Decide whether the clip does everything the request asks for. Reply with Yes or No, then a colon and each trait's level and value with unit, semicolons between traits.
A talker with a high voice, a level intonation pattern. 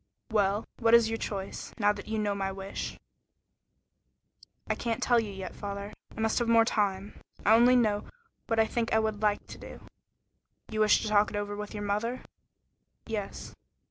Yes: high, 210 Hz; narrow, 1.7 semitones